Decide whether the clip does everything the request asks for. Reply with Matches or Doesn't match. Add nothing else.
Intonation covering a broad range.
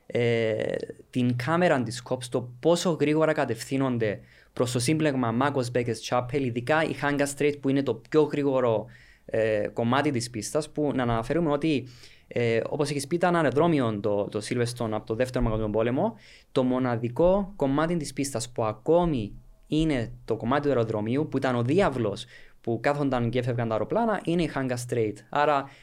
Doesn't match